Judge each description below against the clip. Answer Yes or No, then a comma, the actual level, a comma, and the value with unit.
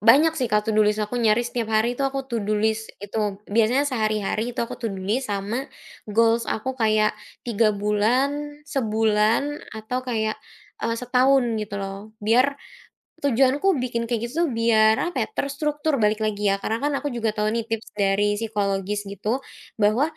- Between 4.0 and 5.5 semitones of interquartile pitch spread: No, average, 3.2 semitones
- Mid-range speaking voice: No, high, 225 Hz